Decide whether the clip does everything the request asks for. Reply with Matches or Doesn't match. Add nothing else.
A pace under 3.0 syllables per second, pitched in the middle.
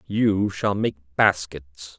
Doesn't match